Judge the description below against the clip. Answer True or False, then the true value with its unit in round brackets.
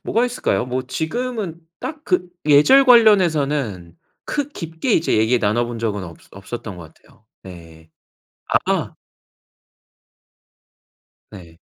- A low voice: True (130 Hz)